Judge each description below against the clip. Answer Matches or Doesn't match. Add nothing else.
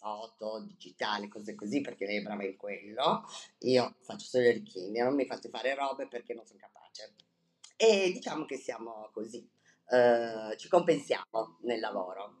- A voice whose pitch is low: Matches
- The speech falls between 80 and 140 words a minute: Doesn't match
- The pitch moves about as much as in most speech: Matches